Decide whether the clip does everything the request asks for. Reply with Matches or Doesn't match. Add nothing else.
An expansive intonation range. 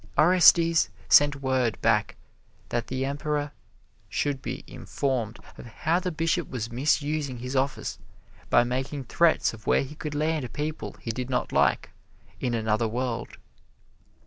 Doesn't match